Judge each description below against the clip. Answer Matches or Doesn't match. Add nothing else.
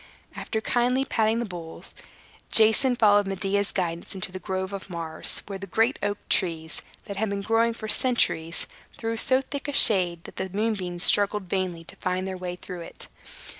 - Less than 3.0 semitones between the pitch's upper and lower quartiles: Doesn't match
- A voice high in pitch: Matches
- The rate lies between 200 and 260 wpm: Doesn't match